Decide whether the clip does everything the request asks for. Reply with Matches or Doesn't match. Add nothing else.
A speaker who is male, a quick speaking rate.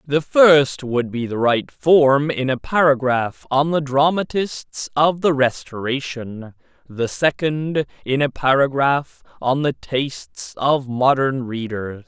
Doesn't match